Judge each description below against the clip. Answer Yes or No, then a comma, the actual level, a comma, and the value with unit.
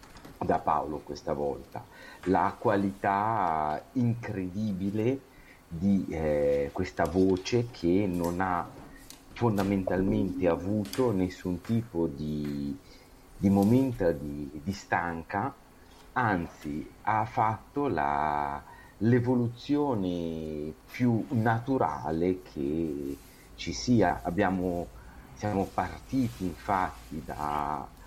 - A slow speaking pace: Yes, slow, 85 wpm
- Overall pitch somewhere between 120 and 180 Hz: No, very low, 95 Hz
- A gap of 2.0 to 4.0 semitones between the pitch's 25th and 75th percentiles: No, average, 5.2 semitones